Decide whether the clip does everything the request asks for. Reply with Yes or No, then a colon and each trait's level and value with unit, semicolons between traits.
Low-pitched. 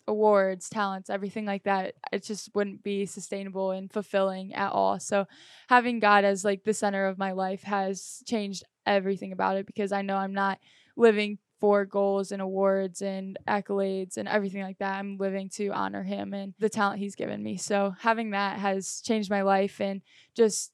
No: high, 195 Hz